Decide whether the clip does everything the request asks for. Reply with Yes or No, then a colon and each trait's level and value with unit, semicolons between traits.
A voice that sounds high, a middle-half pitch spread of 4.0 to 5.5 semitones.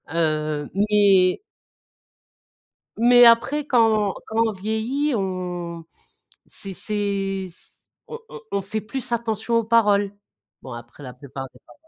Yes: high, 205 Hz; average, 4.4 semitones